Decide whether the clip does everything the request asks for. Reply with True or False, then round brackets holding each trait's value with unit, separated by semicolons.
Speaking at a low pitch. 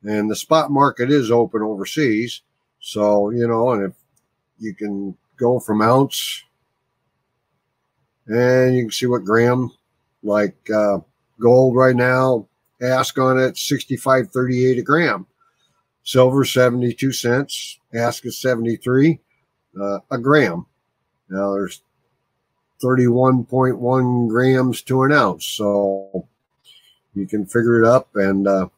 True (120 Hz)